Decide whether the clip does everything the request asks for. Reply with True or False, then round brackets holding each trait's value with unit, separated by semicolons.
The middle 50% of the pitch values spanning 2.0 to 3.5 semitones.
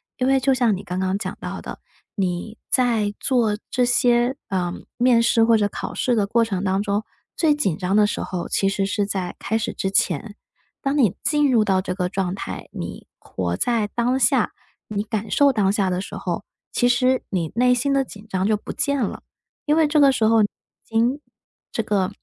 False (4.3 semitones)